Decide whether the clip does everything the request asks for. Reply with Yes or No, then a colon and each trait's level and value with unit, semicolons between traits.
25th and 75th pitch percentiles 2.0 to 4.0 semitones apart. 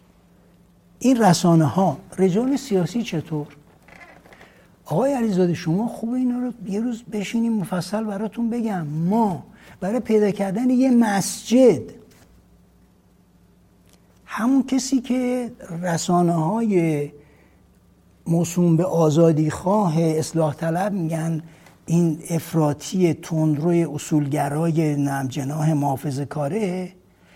No: wide, 5.6 semitones